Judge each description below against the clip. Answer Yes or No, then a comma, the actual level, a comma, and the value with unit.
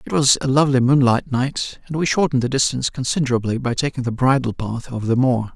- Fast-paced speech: Yes, fast, 215 wpm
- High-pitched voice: No, low, 130 Hz